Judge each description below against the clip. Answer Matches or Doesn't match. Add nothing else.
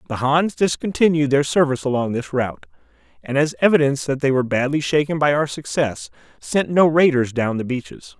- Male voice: Matches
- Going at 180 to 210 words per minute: Matches